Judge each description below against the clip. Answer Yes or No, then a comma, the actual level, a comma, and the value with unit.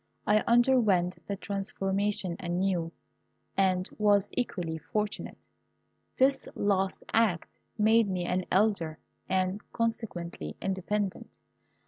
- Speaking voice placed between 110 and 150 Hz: No, high, 195 Hz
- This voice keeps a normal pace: No, slow, 95 wpm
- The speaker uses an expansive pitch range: No, average, 2.7 semitones